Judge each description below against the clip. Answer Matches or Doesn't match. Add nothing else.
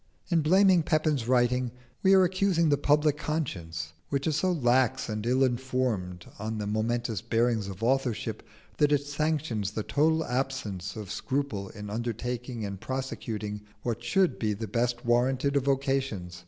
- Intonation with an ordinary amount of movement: Matches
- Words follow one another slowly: Doesn't match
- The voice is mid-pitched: Doesn't match